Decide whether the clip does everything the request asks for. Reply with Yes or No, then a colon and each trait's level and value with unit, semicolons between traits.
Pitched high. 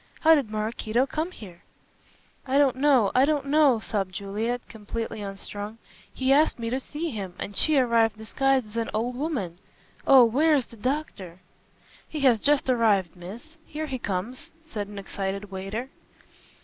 Yes: high, 235 Hz